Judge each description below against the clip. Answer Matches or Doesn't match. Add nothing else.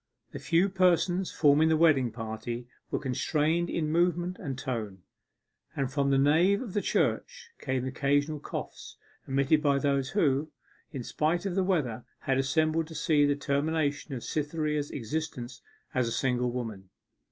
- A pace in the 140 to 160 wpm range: Matches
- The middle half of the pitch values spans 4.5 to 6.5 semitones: Doesn't match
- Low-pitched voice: Doesn't match